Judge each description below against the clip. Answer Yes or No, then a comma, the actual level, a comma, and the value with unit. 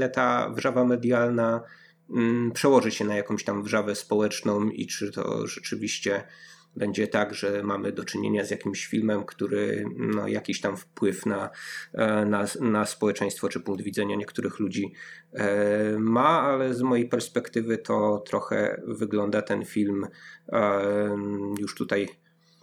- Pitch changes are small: Yes, narrow, 2.3 semitones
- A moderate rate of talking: Yes, average, 130 wpm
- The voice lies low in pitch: Yes, low, 105 Hz